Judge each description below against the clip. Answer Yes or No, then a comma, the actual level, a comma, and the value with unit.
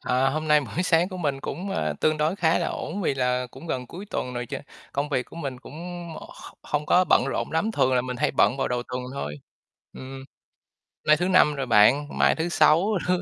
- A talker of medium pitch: Yes, medium, 145 Hz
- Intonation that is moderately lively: Yes, average, 4.5 semitones